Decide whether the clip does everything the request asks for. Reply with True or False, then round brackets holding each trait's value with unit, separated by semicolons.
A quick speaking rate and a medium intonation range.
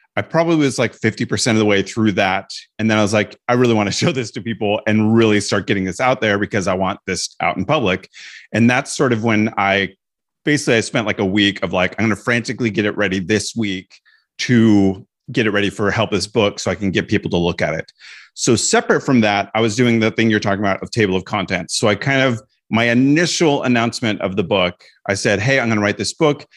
True (255 wpm; 3.1 semitones)